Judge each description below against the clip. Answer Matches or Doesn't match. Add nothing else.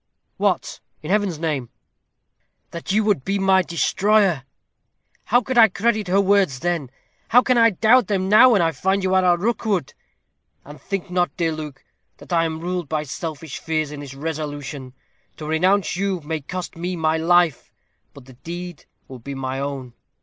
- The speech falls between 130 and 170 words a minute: Doesn't match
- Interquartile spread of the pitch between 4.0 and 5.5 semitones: Matches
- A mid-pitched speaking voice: Matches